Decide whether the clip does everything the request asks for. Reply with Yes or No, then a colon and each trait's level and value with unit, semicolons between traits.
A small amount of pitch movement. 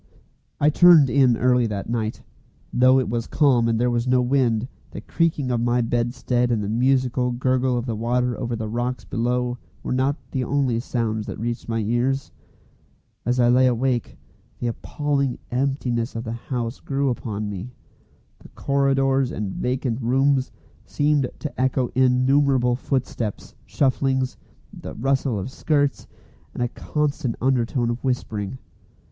Yes: narrow, 2.2 semitones